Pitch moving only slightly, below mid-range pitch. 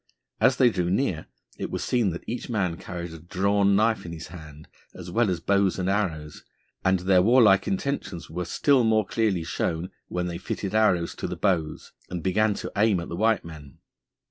No: average, 3.9 semitones; very low, 95 Hz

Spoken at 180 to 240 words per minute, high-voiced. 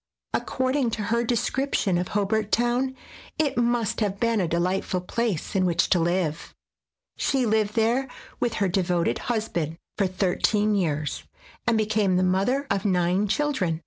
No: average, 160 wpm; high, 205 Hz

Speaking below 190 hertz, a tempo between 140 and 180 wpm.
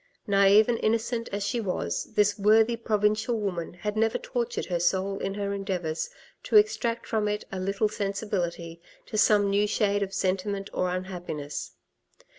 No: high, 200 Hz; average, 160 wpm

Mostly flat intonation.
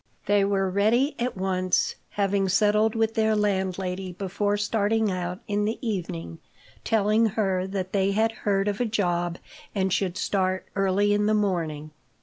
Yes: narrow, 2.2 semitones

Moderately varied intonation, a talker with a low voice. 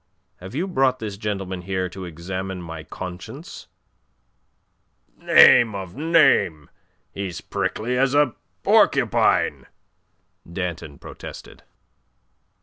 No: wide, 6.1 semitones; very low, 95 Hz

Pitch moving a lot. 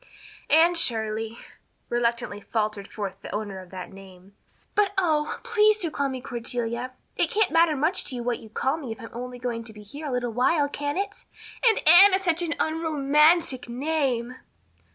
Yes: wide, 6.0 semitones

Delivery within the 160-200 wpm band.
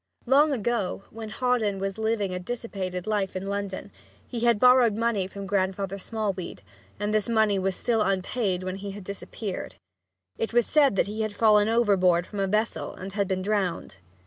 Yes: average, 180 wpm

